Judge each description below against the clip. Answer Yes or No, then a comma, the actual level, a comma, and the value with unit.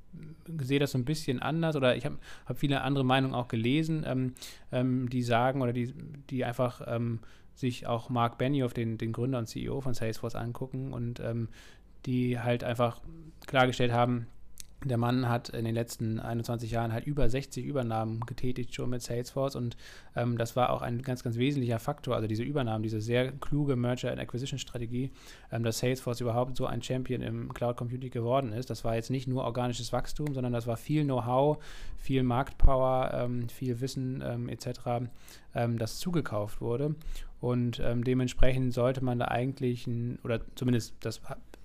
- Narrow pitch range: Yes, narrow, 1.7 semitones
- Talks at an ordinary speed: Yes, average, 180 wpm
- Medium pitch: No, low, 125 Hz